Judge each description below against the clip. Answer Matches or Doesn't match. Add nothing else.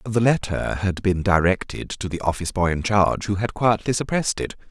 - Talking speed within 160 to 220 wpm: Matches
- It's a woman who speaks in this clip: Doesn't match